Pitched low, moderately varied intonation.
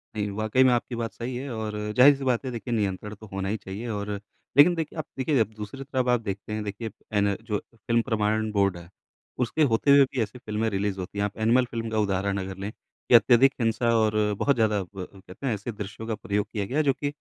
Yes: low, 110 Hz; average, 3.2 semitones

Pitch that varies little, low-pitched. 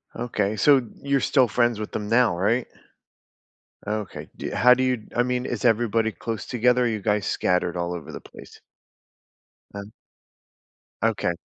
No: average, 3.2 semitones; low, 115 Hz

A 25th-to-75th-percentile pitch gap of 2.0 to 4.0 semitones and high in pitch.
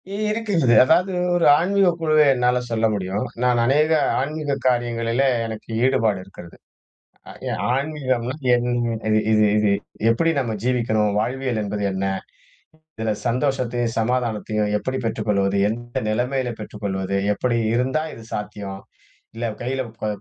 No: average, 3.6 semitones; low, 120 Hz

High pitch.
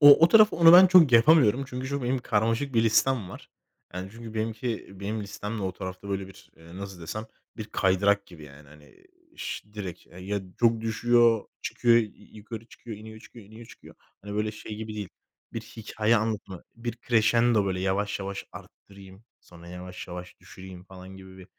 No: low, 105 Hz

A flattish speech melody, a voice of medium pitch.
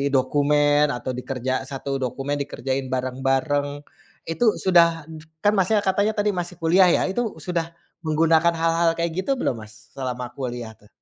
No: average, 4.7 semitones; medium, 145 Hz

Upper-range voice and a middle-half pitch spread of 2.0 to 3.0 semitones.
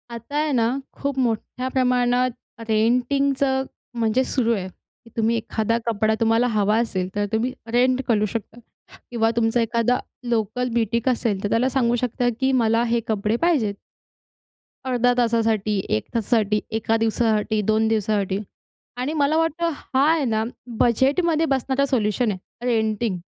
Yes: high, 235 Hz; average, 2.7 semitones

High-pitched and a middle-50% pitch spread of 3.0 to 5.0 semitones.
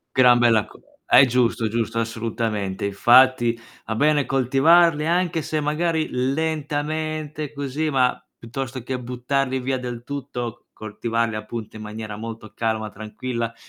No: low, 125 Hz; average, 4.2 semitones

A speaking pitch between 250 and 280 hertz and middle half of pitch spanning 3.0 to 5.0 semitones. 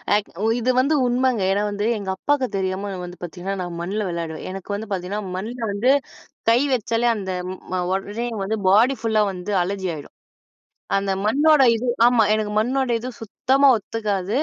No: high, 210 Hz; average, 4.0 semitones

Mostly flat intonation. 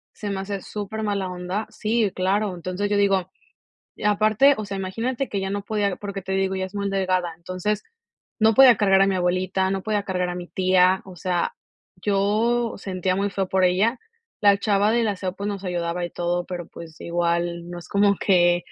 Yes: narrow, 2.1 semitones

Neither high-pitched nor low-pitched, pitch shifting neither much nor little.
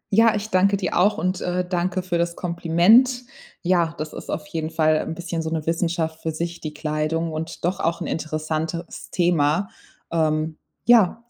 No: medium, 170 Hz; narrow, 2.3 semitones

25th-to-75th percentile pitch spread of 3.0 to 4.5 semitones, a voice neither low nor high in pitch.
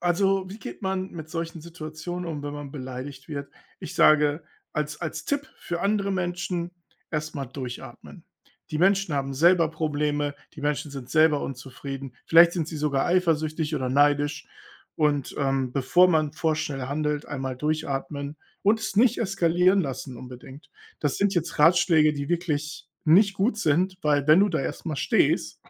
Yes: average, 3.5 semitones; medium, 155 Hz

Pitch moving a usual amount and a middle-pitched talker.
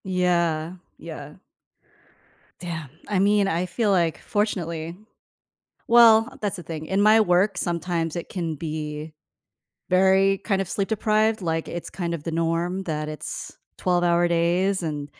Yes: average, 3.0 semitones; medium, 175 Hz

